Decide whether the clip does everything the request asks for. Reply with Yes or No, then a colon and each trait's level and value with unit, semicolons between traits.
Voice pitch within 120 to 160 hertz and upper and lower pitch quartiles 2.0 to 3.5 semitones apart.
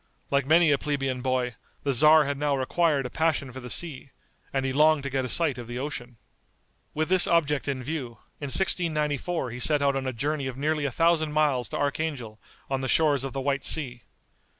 Yes: medium, 140 Hz; average, 2.9 semitones